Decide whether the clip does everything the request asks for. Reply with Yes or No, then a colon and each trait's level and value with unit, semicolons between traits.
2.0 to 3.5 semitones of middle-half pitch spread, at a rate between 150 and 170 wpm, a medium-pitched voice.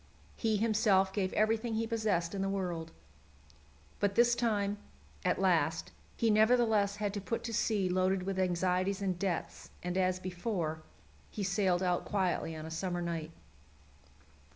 No: average, 3.1 semitones; average, 155 wpm; high, 195 Hz